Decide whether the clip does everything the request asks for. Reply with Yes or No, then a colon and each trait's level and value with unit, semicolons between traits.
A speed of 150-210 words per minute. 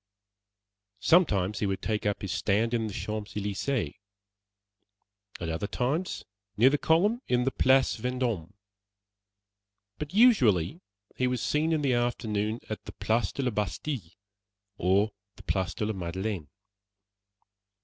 No: average, 140 wpm